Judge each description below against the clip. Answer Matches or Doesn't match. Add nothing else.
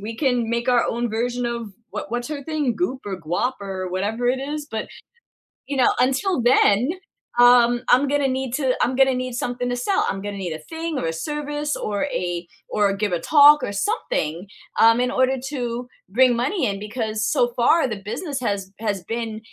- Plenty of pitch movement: Doesn't match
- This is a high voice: Matches